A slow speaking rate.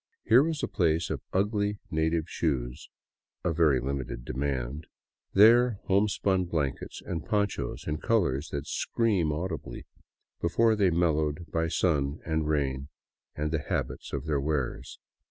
No: average, 150 wpm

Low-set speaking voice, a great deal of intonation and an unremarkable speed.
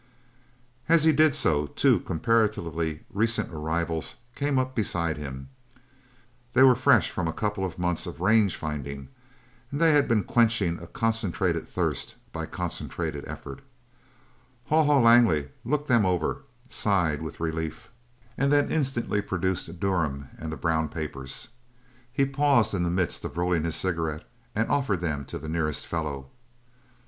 Yes: very low, 90 Hz; wide, 6.7 semitones; average, 150 wpm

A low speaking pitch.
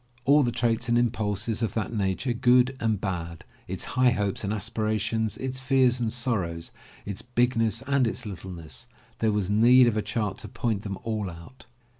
Yes: low, 110 Hz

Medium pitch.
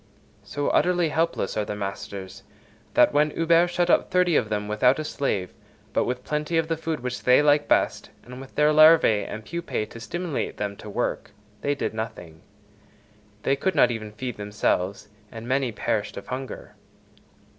No: low, 130 Hz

